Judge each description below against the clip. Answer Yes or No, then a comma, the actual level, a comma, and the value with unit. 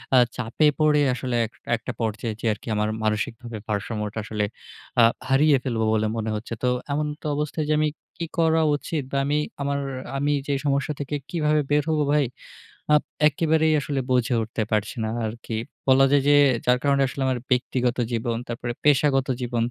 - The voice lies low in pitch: Yes, low, 130 Hz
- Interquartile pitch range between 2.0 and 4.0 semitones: No, average, 4.5 semitones